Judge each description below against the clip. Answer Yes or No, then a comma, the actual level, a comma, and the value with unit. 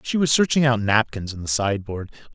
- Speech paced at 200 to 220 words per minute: Yes, fast, 205 wpm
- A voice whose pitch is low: Yes, low, 115 Hz